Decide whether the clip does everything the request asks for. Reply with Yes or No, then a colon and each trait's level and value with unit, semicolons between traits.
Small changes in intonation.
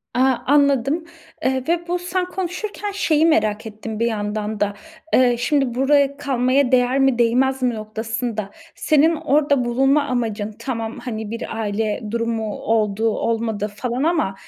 No: average, 4.3 semitones